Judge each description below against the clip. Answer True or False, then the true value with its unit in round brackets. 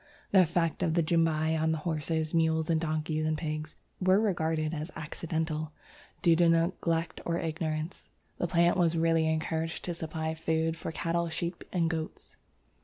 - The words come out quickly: False (155 wpm)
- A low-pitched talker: False (160 Hz)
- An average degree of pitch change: False (1.2 semitones)